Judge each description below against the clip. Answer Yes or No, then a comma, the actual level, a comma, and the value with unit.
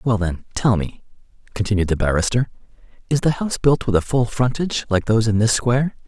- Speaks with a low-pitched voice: Yes, low, 115 Hz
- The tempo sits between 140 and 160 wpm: No, average, 195 wpm